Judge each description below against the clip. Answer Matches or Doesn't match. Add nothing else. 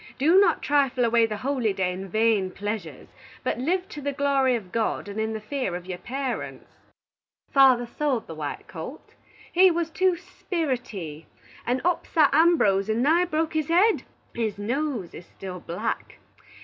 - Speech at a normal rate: Matches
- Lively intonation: Matches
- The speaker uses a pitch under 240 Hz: Doesn't match